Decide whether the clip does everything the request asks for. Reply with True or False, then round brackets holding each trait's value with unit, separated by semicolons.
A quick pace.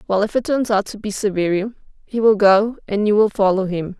True (240 wpm)